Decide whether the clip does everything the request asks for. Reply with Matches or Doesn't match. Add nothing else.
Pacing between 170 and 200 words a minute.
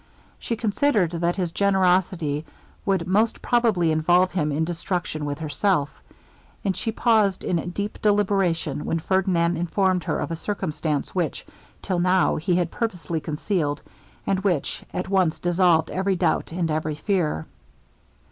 Doesn't match